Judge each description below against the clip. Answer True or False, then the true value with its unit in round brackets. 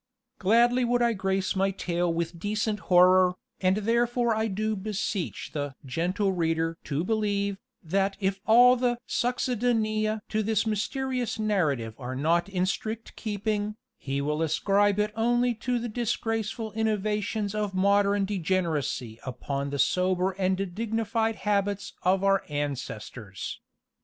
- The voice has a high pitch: True (200 Hz)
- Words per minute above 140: False (135 wpm)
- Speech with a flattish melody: False (3.7 semitones)